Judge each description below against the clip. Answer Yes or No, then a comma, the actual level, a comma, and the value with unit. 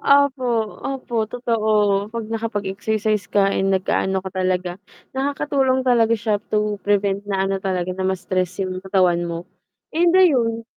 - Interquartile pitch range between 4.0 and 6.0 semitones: No, average, 3.4 semitones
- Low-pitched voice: No, high, 205 Hz